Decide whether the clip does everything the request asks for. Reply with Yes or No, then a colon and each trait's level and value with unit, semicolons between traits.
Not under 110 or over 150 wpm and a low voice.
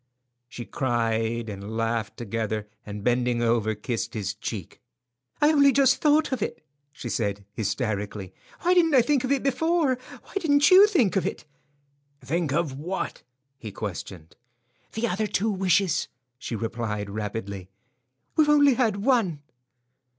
Yes: average, 145 wpm; low, 125 Hz